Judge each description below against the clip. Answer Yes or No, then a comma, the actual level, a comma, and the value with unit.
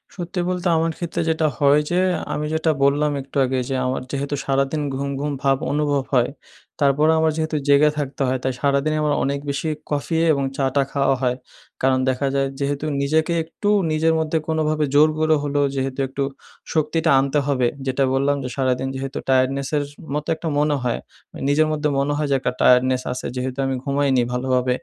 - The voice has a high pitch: No, medium, 140 Hz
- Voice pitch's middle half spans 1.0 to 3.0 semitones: Yes, narrow, 2.5 semitones